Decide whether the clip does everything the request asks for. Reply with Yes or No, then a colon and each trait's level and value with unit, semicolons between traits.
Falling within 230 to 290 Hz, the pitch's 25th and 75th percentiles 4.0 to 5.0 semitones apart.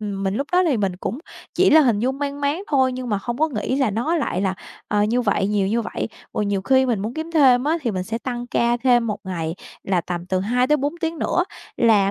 No: high, 240 Hz; wide, 5.6 semitones